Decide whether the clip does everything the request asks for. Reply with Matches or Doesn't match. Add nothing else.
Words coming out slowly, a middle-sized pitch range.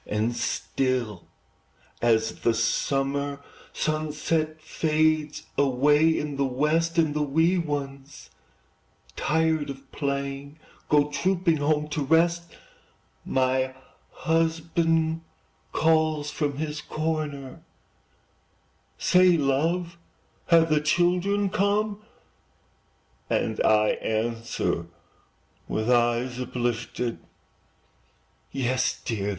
Matches